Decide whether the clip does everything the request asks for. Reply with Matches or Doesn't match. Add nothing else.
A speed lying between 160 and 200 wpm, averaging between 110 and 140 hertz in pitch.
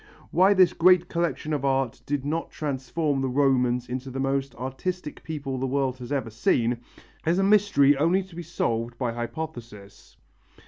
Matches